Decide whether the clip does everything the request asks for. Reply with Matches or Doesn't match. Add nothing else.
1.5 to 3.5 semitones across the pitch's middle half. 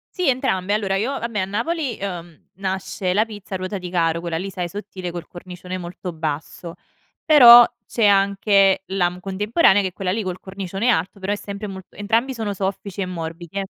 Matches